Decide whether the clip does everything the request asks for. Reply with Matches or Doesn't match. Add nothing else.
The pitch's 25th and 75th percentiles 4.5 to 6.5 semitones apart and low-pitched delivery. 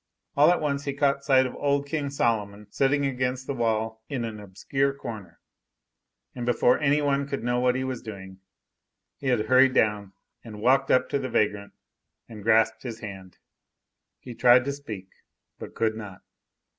Doesn't match